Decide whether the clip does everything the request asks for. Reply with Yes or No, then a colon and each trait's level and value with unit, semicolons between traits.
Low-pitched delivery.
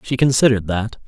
Yes: low, 115 Hz